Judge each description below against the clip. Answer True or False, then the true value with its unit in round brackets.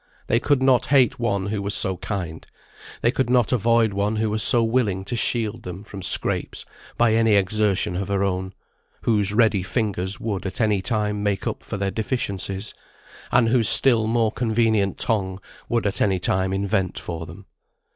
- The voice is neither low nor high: False (105 Hz)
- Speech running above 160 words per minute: True (180 wpm)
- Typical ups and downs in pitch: True (3.0 semitones)